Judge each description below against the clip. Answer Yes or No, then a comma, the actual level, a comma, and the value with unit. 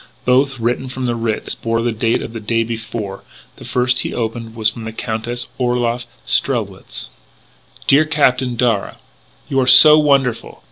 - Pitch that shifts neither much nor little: No, narrow, 2.0 semitones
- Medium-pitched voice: No, low, 120 Hz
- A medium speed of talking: Yes, average, 170 wpm